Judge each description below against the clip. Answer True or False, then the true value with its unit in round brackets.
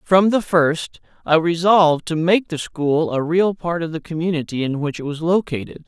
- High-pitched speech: False (165 Hz)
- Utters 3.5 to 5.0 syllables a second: True (4.9 syllables/s)